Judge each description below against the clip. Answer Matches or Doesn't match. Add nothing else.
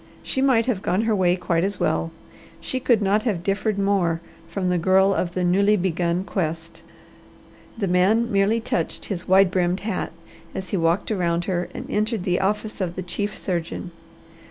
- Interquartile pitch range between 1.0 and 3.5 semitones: Matches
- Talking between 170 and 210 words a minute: Matches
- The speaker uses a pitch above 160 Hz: Matches